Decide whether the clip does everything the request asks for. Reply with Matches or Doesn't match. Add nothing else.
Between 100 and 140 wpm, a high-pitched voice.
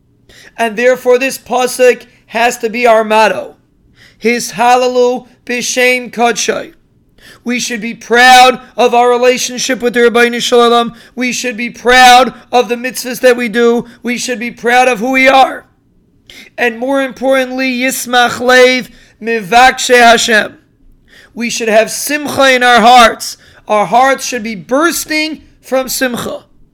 Matches